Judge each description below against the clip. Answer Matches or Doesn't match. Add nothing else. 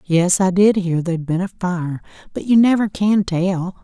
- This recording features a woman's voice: Matches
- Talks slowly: Doesn't match